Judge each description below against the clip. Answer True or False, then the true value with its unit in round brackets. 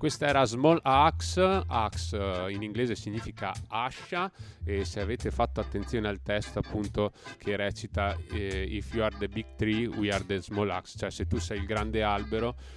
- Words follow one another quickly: True (185 wpm)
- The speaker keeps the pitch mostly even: True (2.3 semitones)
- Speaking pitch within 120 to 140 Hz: False (105 Hz)